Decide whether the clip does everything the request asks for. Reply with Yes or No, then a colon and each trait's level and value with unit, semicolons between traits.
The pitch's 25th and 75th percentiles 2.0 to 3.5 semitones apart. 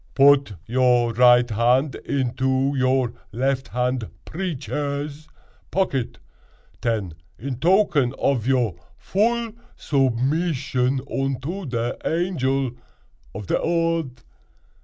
Yes: average, 3.1 semitones